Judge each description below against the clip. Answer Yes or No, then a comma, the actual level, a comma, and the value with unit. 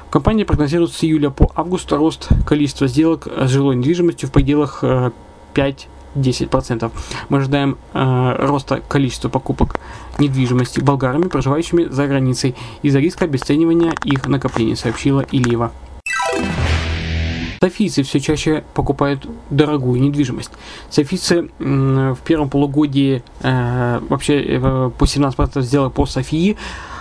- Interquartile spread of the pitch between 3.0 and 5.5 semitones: No, narrow, 2.6 semitones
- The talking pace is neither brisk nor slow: No, slow, 105 wpm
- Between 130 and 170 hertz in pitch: Yes, medium, 140 Hz